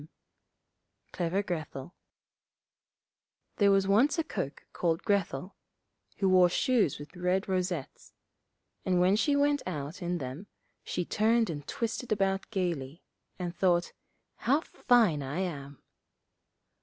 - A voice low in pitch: No, medium, 185 Hz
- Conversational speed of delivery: No, slow, 125 wpm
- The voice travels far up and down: No, average, 3.7 semitones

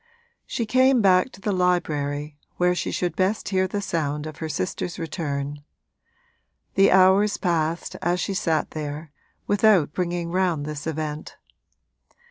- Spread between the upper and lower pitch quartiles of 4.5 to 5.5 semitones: No, average, 3.7 semitones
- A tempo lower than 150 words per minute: Yes, average, 140 wpm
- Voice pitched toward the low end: No, medium, 175 Hz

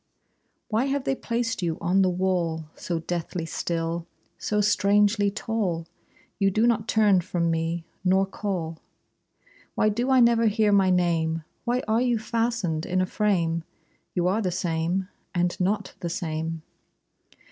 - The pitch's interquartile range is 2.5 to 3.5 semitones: No, average, 4.3 semitones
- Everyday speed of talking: Yes, average, 150 wpm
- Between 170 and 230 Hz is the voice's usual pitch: Yes, high, 190 Hz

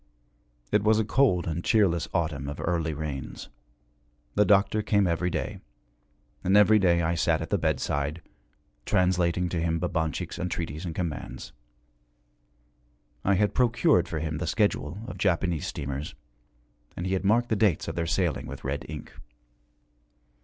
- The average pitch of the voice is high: No, very low, 85 Hz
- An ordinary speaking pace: Yes, average, 155 wpm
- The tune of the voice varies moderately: Yes, average, 3.8 semitones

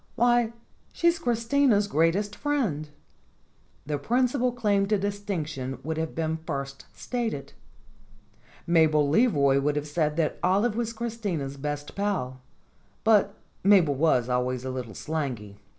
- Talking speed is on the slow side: Yes, slow, 130 wpm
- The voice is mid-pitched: Yes, medium, 165 Hz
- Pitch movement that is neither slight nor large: No, wide, 7.5 semitones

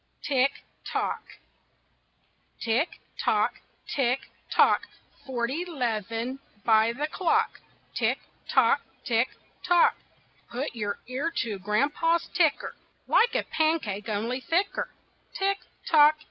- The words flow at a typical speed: No, slow, 105 wpm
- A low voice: No, very high, 265 Hz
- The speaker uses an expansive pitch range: Yes, wide, 6.2 semitones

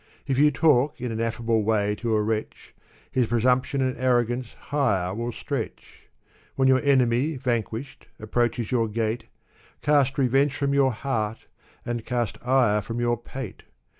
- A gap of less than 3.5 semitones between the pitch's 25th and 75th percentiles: Yes, average, 2.8 semitones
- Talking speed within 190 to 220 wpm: No, average, 150 wpm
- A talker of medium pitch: No, low, 120 Hz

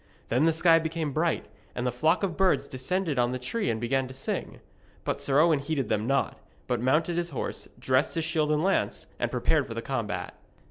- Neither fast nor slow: No, fast, 215 wpm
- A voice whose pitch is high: No, medium, 150 Hz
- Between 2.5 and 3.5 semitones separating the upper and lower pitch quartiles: No, average, 4.3 semitones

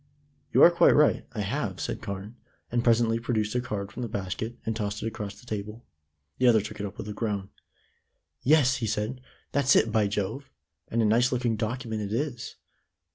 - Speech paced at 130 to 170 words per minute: No, average, 200 wpm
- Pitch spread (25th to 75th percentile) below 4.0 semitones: Yes, average, 2.8 semitones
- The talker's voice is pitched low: Yes, low, 110 Hz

